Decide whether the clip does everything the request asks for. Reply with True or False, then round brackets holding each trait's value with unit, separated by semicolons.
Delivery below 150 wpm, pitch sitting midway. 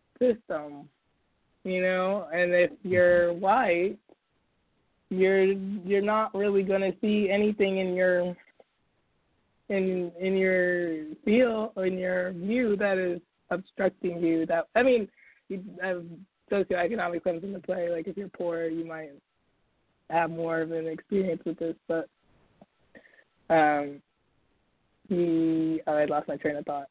True (135 wpm; 180 Hz)